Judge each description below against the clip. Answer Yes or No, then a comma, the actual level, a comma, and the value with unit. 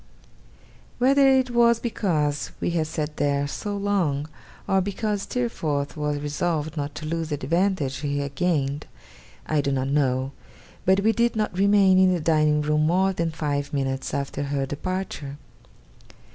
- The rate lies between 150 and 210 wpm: Yes, average, 160 wpm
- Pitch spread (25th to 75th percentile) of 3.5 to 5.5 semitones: Yes, average, 5.2 semitones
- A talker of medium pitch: Yes, medium, 155 Hz